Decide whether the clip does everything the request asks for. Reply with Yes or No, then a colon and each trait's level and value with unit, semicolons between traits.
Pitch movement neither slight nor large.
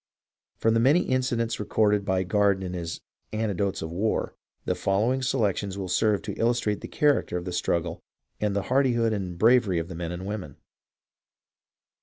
Yes: average, 4.0 semitones